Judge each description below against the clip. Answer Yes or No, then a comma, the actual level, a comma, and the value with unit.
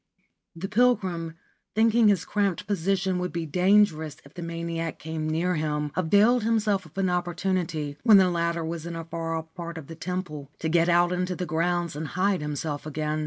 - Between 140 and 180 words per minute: No, average, 200 wpm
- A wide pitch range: No, average, 2.8 semitones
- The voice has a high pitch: No, medium, 170 Hz